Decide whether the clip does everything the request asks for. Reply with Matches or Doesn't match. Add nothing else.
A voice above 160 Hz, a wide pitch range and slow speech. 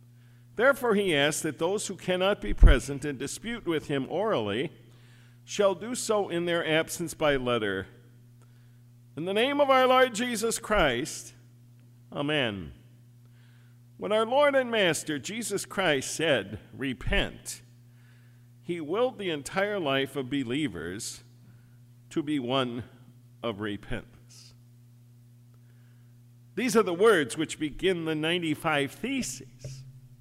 Doesn't match